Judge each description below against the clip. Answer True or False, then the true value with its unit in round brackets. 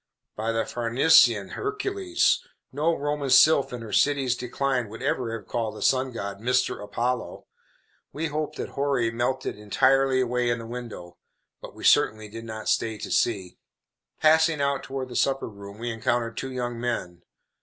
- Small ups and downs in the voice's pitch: False (3.2 semitones)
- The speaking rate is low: False (165 wpm)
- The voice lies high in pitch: False (125 Hz)